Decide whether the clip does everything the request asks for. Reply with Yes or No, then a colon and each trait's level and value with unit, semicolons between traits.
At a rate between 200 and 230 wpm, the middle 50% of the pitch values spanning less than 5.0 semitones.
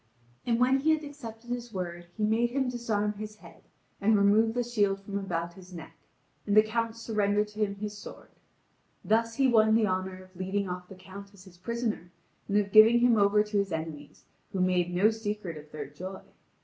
Yes: fast, 205 wpm; average, 3.3 semitones